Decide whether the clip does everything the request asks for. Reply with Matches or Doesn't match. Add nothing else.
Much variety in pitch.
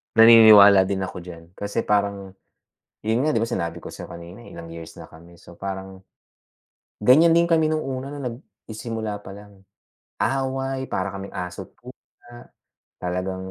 Doesn't match